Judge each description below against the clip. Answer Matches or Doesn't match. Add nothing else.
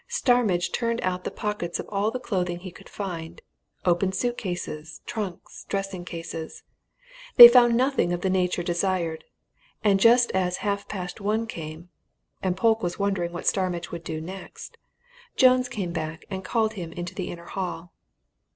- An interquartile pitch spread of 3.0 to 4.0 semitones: Matches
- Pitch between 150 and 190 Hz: Matches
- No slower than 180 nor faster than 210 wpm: Doesn't match